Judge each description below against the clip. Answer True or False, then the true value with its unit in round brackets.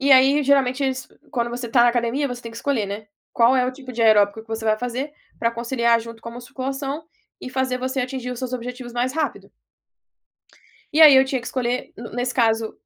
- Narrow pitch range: True (2.1 semitones)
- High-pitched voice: True (250 Hz)